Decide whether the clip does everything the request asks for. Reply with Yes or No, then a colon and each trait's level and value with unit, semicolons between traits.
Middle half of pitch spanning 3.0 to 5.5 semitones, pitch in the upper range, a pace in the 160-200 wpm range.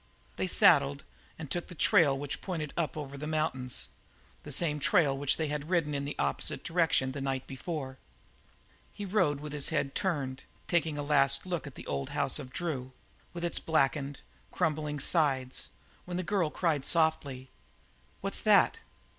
No: average, 3.3 semitones; medium, 150 Hz; average, 170 wpm